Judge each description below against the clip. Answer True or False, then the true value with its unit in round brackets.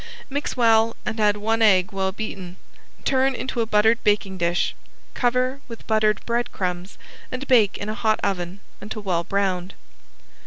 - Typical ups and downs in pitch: True (3.3 semitones)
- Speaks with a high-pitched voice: True (215 Hz)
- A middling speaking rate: True (155 wpm)